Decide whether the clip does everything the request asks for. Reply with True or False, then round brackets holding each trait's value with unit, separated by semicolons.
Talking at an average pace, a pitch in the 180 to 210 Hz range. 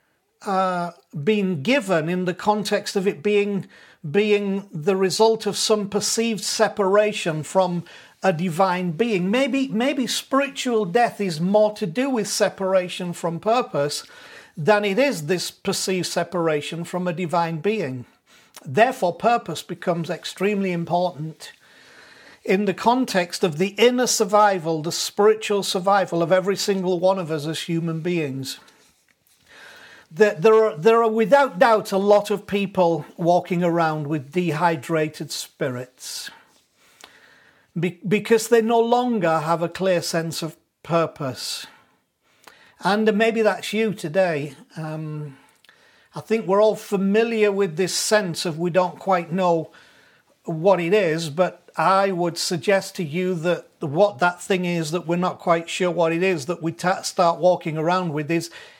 True (145 wpm; 185 Hz)